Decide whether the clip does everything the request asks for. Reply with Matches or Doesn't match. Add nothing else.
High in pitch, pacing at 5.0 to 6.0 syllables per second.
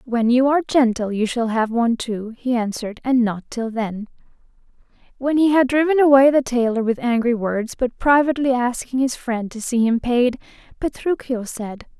Matches